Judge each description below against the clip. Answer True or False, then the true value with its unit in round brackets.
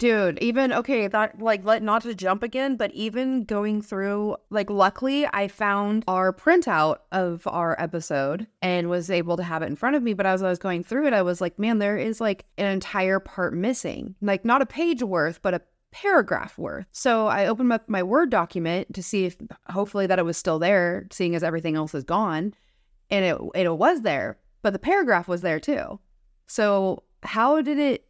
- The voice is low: False (200 Hz)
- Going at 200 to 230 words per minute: True (205 wpm)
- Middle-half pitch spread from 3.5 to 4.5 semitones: True (4.1 semitones)